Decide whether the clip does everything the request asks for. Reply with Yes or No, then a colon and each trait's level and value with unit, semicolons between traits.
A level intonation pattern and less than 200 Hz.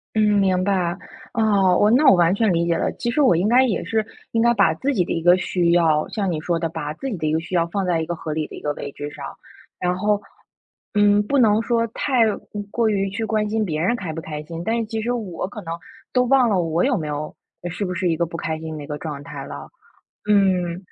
No: average, 4.7 semitones; medium, 185 Hz